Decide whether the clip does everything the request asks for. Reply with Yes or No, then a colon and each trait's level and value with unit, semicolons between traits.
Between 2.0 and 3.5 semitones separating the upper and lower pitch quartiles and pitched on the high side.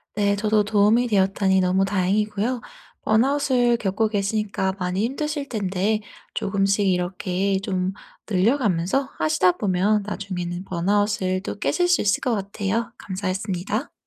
Yes: narrow, 2.5 semitones; high, 200 Hz